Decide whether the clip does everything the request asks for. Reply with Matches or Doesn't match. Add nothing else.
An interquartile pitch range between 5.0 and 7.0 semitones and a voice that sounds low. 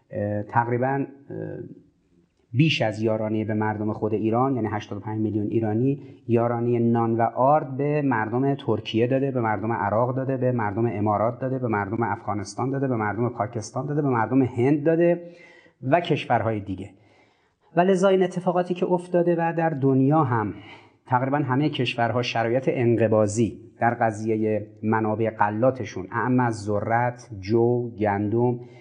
Doesn't match